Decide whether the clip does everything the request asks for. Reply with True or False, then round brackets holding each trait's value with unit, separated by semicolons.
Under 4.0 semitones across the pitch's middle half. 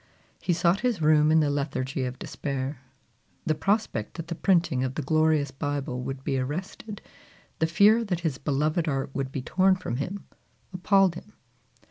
False (4.9 semitones)